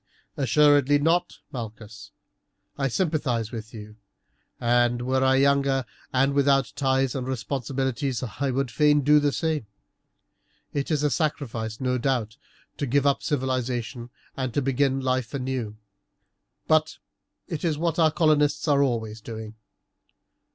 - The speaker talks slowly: Yes, slow, 130 wpm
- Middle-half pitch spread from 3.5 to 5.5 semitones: No, average, 3.1 semitones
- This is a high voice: No, low, 135 Hz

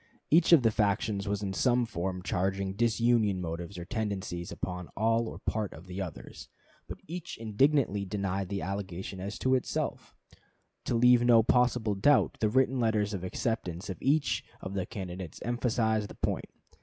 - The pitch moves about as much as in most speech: Yes, average, 3.9 semitones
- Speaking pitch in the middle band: No, low, 105 Hz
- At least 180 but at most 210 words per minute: No, average, 170 wpm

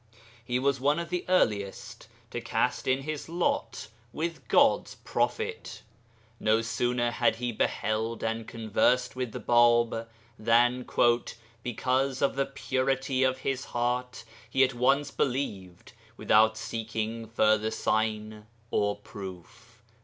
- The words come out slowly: Yes, slow, 125 wpm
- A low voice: Yes, low, 120 Hz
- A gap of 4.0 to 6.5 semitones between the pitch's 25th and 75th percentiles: No, average, 3.1 semitones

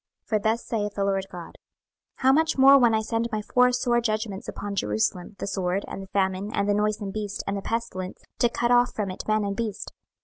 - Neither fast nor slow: No, fast, 230 wpm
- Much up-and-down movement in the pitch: No, average, 3.0 semitones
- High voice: Yes, high, 210 Hz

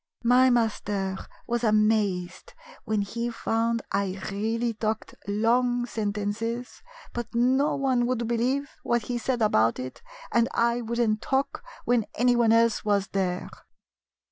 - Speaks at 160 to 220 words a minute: No, slow, 135 wpm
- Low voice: No, high, 230 Hz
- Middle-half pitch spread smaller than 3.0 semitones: Yes, narrow, 2.5 semitones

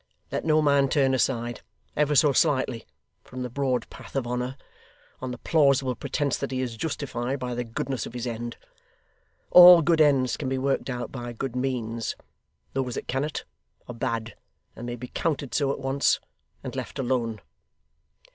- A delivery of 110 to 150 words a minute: No, average, 175 wpm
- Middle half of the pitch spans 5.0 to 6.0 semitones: No, narrow, 2.4 semitones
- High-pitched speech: No, low, 130 Hz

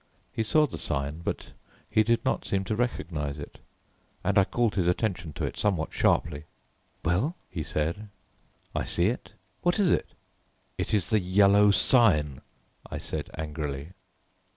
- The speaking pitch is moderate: No, very low, 95 Hz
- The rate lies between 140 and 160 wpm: Yes, average, 155 wpm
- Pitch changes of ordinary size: No, wide, 5.8 semitones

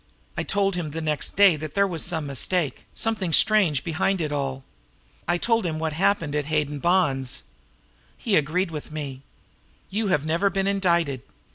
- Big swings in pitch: No, average, 4.5 semitones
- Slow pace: No, average, 165 wpm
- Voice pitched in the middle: Yes, medium, 165 Hz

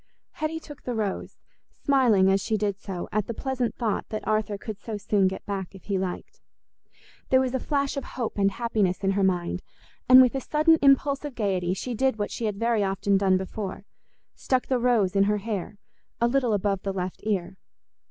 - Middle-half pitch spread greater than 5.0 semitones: No, average, 4.4 semitones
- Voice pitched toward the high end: Yes, high, 210 Hz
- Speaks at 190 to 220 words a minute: Yes, average, 200 wpm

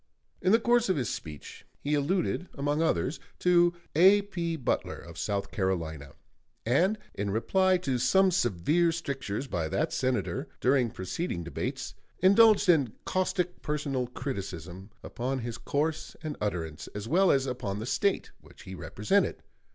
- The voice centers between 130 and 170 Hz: Yes, medium, 140 Hz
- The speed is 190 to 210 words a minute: No, average, 145 wpm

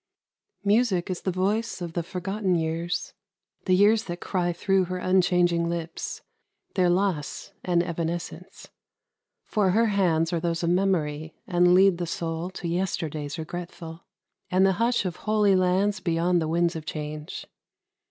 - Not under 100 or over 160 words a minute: Yes, average, 150 wpm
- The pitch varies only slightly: Yes, narrow, 2.2 semitones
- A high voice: No, medium, 175 Hz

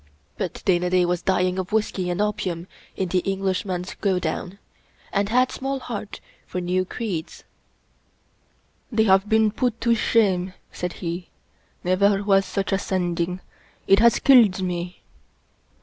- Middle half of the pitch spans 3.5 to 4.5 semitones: No, average, 2.7 semitones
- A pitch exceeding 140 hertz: Yes, high, 190 Hz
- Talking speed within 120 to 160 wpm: Yes, average, 150 wpm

